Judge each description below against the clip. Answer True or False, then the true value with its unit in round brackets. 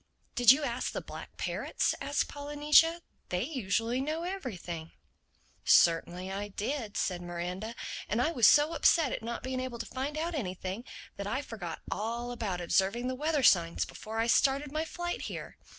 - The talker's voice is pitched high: True (240 Hz)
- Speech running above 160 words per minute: True (170 wpm)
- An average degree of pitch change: False (6.6 semitones)